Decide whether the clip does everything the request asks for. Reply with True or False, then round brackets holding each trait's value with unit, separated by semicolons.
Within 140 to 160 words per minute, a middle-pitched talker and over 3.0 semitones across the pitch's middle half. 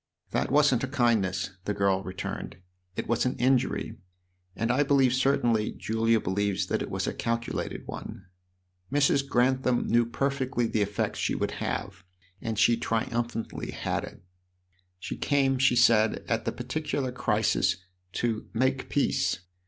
False (145 wpm; 120 Hz; 3.4 semitones)